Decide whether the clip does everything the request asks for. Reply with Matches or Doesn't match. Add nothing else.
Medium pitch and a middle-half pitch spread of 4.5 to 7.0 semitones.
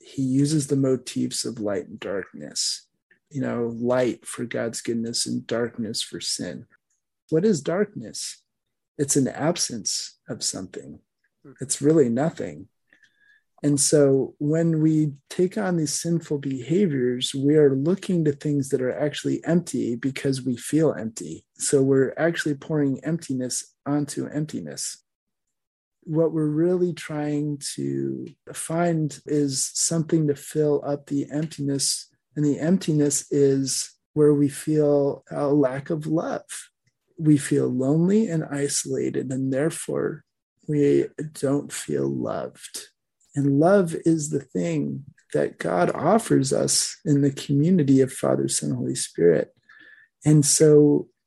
Doesn't match